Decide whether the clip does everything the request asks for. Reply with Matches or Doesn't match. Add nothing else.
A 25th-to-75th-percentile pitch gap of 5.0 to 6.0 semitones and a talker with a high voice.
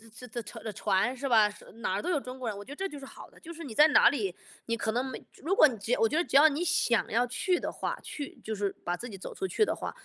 Matches